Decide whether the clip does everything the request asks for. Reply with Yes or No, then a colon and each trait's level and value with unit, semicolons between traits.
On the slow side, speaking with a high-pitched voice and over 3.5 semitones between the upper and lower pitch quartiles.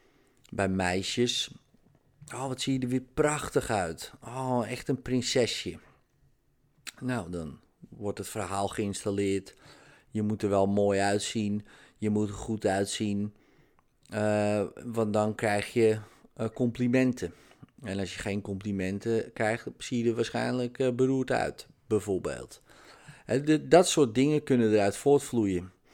No: slow, 130 wpm; low, 110 Hz; average, 4.0 semitones